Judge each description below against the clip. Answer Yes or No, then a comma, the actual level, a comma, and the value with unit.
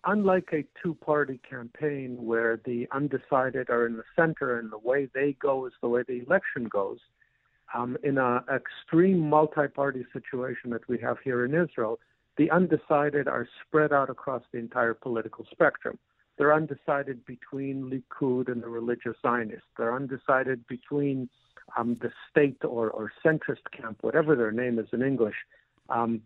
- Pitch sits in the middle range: No, low, 130 Hz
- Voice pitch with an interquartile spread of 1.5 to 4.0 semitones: Yes, average, 3.5 semitones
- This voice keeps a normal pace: Yes, average, 160 wpm